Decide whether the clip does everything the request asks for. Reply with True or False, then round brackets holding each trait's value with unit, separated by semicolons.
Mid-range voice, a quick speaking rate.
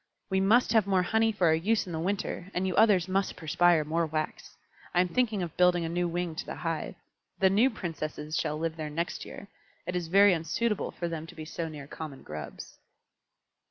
True (175 Hz; 215 wpm)